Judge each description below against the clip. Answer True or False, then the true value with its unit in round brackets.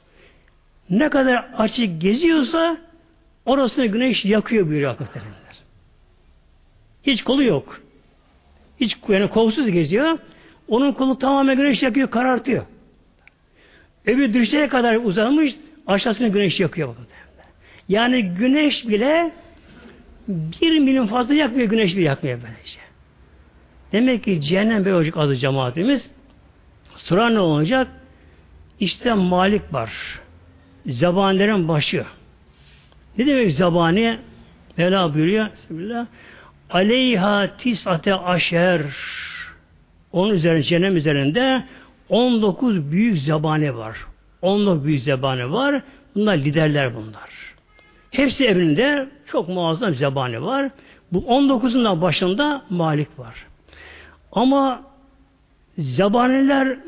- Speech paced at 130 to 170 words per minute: False (95 wpm)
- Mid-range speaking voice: False (200 Hz)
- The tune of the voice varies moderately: False (8.7 semitones)